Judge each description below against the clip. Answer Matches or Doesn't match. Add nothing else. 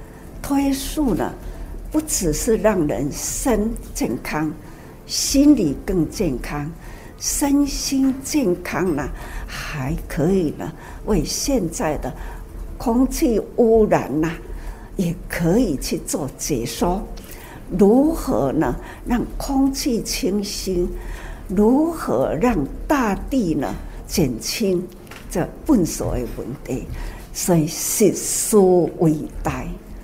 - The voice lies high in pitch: Matches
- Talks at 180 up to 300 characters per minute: Doesn't match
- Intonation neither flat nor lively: Doesn't match